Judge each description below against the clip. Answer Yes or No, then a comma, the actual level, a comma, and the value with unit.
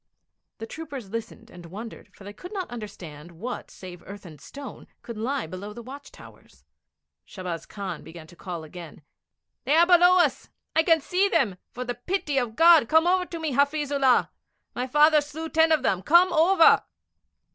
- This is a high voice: Yes, very high, 255 Hz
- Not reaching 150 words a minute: No, average, 185 wpm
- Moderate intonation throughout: No, wide, 8.3 semitones